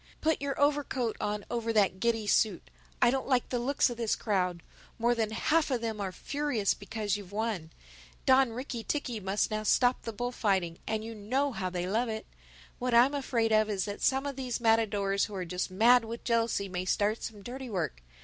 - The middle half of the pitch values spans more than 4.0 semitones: No, average, 3.4 semitones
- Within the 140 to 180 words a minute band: No, average, 200 wpm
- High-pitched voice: Yes, high, 225 Hz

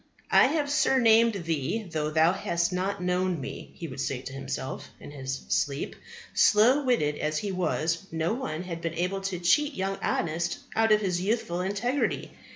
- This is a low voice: No, medium, 180 Hz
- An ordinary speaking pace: Yes, average, 175 wpm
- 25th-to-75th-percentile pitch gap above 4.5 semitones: Yes, average, 5.1 semitones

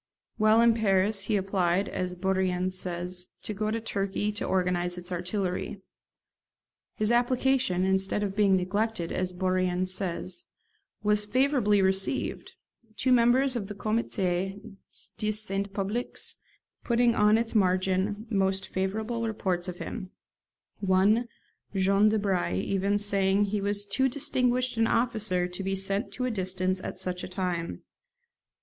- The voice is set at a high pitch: Yes, high, 195 Hz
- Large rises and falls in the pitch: No, average, 2.8 semitones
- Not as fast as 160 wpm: Yes, average, 140 wpm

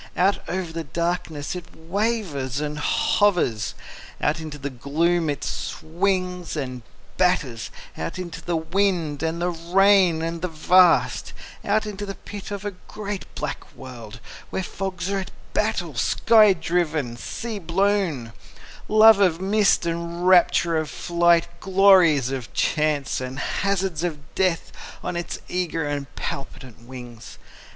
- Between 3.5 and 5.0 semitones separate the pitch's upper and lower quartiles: Yes, average, 4.4 semitones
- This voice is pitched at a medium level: Yes, medium, 170 Hz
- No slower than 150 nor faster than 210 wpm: No, average, 140 wpm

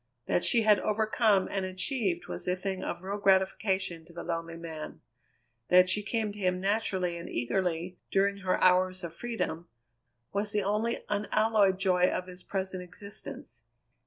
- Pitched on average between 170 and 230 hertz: Yes, high, 190 Hz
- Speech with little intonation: Yes, narrow, 2.3 semitones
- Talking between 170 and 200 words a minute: No, average, 160 wpm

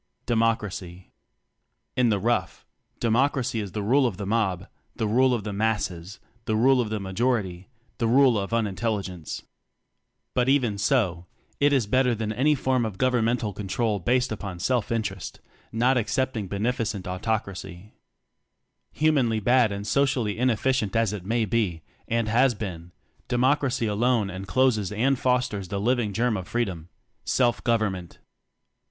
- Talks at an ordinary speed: Yes, average, 160 wpm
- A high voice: No, low, 110 Hz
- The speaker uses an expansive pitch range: No, average, 3.9 semitones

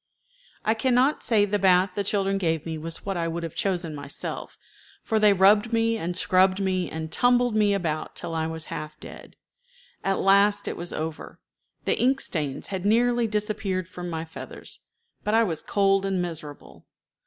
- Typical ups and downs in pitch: Yes, average, 4.1 semitones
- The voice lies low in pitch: No, high, 195 Hz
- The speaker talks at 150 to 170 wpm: No, average, 185 wpm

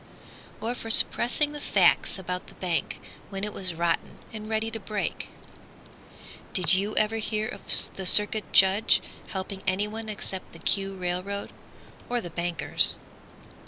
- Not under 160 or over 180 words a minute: No, average, 145 wpm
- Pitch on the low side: No, high, 200 Hz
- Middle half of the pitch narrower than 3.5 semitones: Yes, average, 2.8 semitones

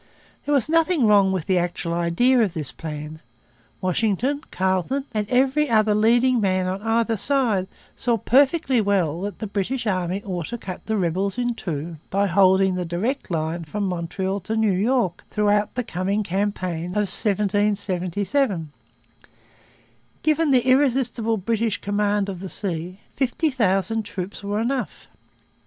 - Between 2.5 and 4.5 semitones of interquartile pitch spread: Yes, average, 4.2 semitones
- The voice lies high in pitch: Yes, high, 205 Hz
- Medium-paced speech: Yes, average, 150 wpm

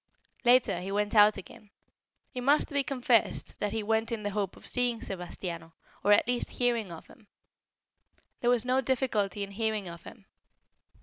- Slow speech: No, average, 175 wpm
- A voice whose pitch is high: Yes, high, 220 Hz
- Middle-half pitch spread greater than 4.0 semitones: No, average, 3.7 semitones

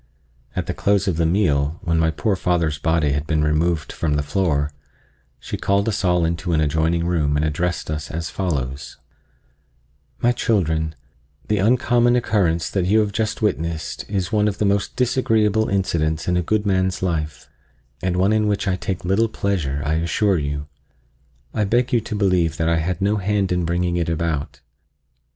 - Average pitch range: Yes, average, 4.2 semitones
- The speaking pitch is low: Yes, very low, 90 Hz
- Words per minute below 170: No, average, 180 wpm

